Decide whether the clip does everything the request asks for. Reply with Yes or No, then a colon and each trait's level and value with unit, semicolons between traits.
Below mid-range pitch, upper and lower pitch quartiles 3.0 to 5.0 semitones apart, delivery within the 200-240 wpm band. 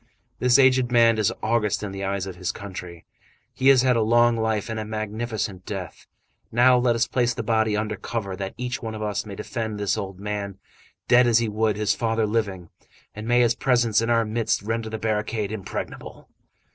No: low, 110 Hz; narrow, 2.4 semitones; fast, 205 wpm